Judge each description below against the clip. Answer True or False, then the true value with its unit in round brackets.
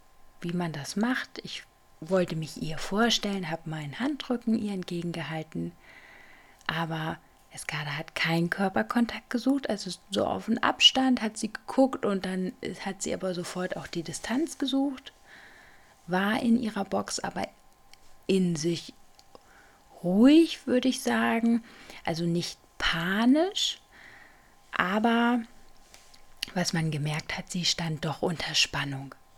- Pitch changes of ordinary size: False (5.9 semitones)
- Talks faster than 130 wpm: False (125 wpm)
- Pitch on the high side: True (195 Hz)